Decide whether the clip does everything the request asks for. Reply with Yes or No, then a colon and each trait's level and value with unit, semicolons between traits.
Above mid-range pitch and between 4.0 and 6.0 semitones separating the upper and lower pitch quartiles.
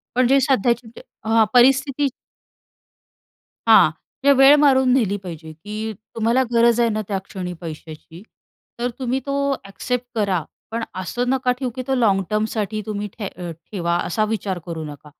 Yes: high, 220 Hz; average, 4.7 semitones